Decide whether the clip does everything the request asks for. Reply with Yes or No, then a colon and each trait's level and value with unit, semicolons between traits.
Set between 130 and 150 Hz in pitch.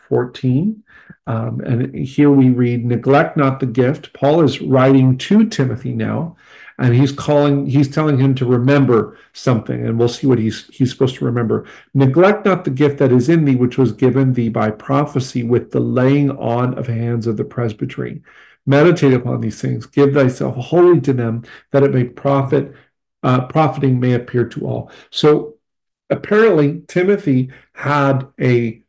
Yes: low, 135 Hz